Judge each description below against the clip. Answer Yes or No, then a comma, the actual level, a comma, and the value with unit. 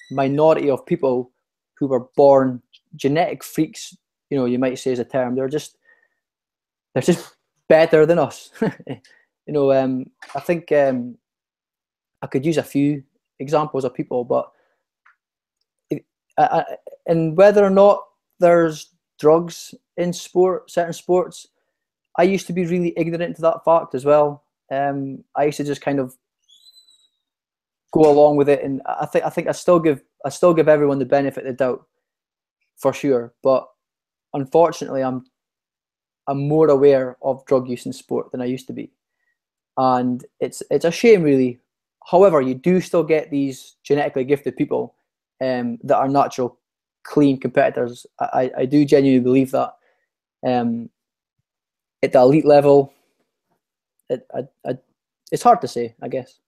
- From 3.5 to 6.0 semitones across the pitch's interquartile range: Yes, average, 4.2 semitones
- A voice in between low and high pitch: Yes, medium, 145 Hz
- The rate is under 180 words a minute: Yes, average, 160 wpm